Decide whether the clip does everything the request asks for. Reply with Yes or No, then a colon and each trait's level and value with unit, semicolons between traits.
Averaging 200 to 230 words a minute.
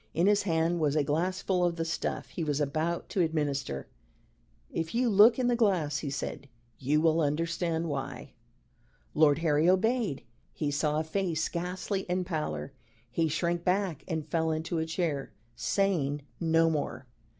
No: average, 165 wpm